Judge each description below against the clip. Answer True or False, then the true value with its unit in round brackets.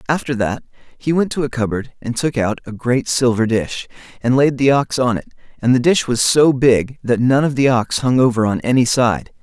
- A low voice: True (125 Hz)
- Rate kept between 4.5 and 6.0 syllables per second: True (5.1 syllables/s)